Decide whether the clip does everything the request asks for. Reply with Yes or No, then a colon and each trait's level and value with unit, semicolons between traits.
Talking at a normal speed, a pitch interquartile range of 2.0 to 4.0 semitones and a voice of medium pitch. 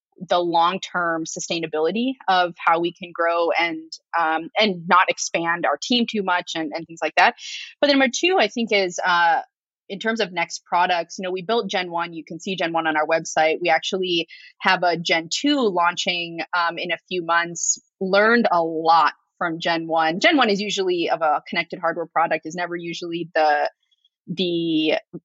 Yes: average, 195 wpm; average, 3.0 semitones; medium, 175 Hz